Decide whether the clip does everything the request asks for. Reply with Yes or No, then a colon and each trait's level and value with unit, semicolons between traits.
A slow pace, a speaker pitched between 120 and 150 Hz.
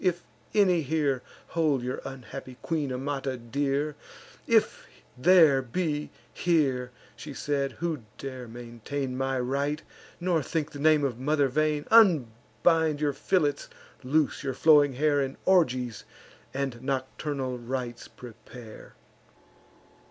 Yes: slow, 120 wpm; medium, 140 Hz